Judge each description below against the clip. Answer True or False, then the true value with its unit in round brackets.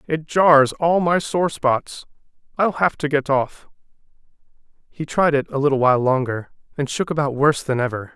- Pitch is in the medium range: True (145 Hz)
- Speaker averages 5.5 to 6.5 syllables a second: False (5.0 syllables/s)